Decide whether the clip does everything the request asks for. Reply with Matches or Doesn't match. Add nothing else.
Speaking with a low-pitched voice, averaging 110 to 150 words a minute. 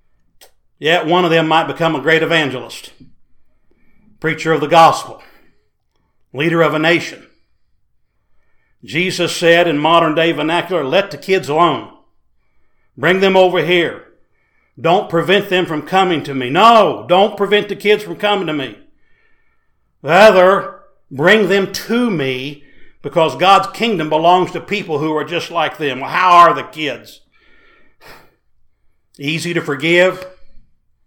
Doesn't match